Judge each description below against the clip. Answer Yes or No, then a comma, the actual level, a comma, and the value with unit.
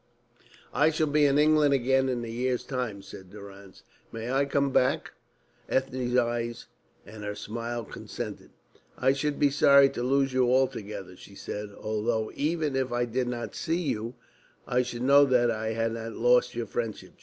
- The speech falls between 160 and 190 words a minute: Yes, average, 175 wpm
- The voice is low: Yes, low, 125 Hz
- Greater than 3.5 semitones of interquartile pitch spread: No, average, 3.2 semitones